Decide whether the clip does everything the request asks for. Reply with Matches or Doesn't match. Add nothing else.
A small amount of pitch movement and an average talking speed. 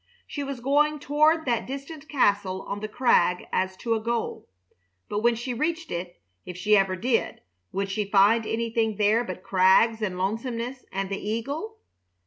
Doesn't match